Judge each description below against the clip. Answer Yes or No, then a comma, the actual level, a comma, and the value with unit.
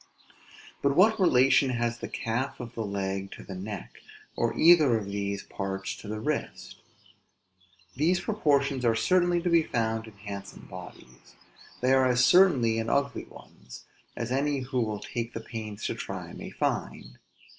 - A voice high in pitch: No, low, 120 Hz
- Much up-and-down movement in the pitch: No, average, 4.9 semitones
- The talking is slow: No, average, 165 wpm